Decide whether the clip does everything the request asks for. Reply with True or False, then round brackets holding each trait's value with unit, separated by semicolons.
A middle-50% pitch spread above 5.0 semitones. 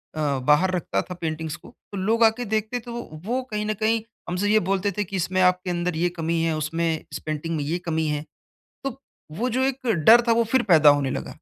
True (5.5 semitones)